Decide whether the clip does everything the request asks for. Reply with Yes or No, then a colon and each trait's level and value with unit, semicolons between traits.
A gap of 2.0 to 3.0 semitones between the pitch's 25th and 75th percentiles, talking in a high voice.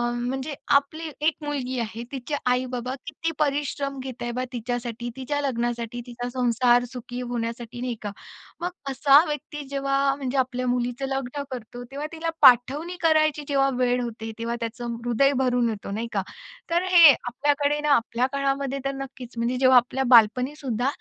Yes: narrow, 2.6 semitones; very high, 255 Hz